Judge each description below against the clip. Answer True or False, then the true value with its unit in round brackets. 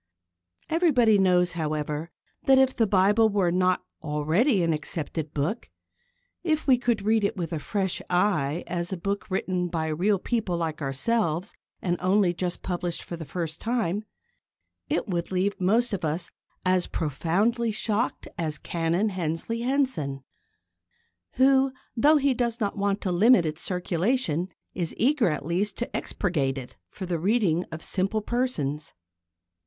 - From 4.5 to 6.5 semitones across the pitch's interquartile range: True (5.1 semitones)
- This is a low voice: False (185 Hz)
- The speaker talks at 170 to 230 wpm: False (150 wpm)